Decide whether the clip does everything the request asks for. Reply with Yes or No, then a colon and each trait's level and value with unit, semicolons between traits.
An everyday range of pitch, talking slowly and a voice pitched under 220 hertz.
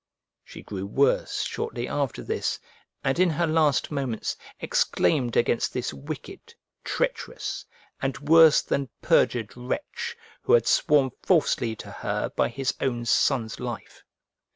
Yes: average, 4.9 semitones; slow, 130 wpm; low, 135 Hz